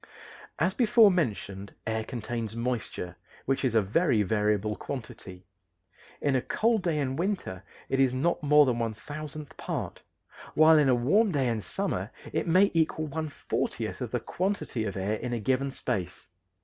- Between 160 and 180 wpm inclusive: Yes, average, 170 wpm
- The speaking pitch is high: No, low, 130 Hz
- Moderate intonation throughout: No, wide, 6.1 semitones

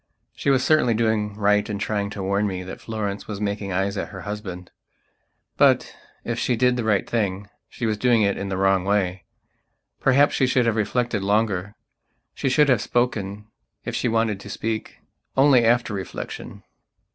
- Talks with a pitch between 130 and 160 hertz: No, low, 105 Hz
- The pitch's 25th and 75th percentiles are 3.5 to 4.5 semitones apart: No, average, 2.8 semitones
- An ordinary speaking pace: Yes, average, 180 wpm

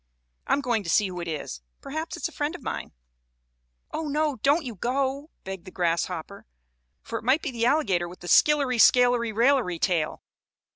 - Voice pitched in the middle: No, high, 240 Hz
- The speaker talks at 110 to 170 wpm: No, average, 190 wpm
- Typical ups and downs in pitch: No, wide, 7.6 semitones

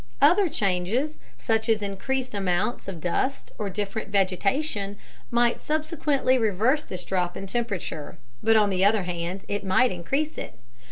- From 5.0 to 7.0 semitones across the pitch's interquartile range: Yes, average, 5.3 semitones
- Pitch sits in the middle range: No, high, 205 Hz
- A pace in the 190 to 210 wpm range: No, average, 150 wpm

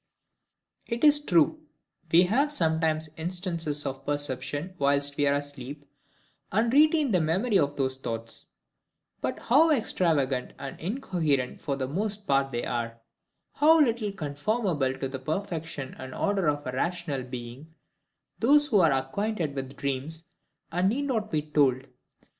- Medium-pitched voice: Yes, medium, 155 Hz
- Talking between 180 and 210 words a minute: No, average, 140 wpm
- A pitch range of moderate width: No, wide, 6.8 semitones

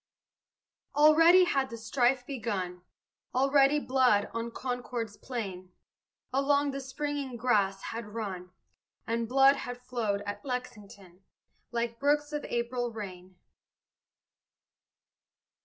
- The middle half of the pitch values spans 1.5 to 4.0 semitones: No, average, 4.6 semitones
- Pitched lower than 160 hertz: No, high, 245 Hz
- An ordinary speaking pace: No, slow, 105 wpm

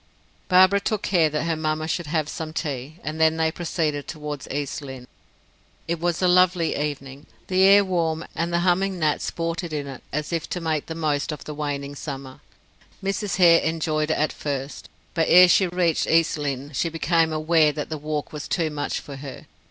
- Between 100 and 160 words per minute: No, average, 200 wpm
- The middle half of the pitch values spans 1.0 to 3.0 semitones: Yes, narrow, 2.5 semitones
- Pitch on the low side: No, medium, 160 Hz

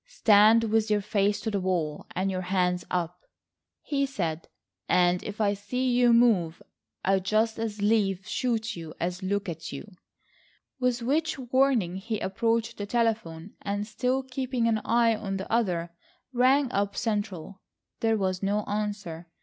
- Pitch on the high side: Yes, high, 210 Hz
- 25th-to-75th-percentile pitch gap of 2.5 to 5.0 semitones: Yes, average, 3.7 semitones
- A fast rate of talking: No, average, 160 wpm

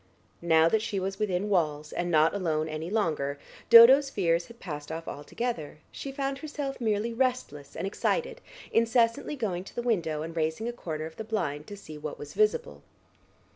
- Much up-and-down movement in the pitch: Yes, wide, 6.8 semitones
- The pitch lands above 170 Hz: Yes, high, 190 Hz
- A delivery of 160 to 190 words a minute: Yes, average, 180 wpm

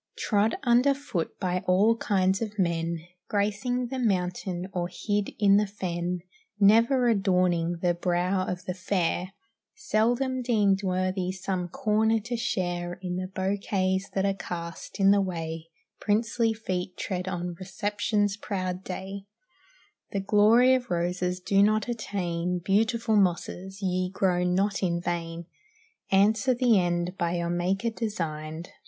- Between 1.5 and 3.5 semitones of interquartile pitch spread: Yes, average, 3.0 semitones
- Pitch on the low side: No, high, 190 Hz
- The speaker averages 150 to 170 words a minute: No, average, 140 wpm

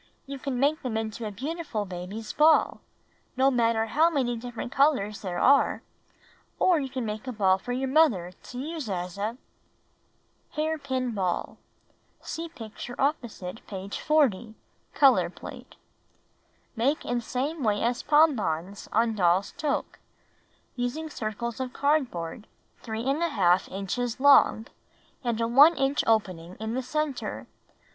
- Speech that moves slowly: No, average, 145 wpm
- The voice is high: Yes, high, 245 Hz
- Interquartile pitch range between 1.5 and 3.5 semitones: No, average, 5.0 semitones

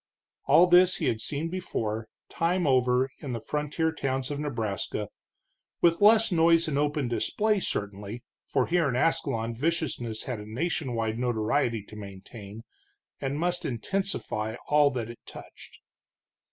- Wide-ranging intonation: Yes, wide, 6.6 semitones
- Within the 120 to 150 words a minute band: Yes, average, 145 wpm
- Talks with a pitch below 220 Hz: Yes, low, 135 Hz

